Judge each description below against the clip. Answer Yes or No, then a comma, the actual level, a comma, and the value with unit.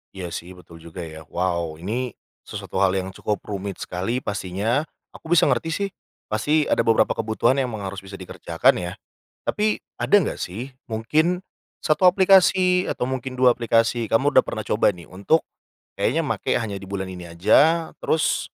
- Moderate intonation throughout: No, wide, 6.9 semitones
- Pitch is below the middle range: Yes, low, 110 Hz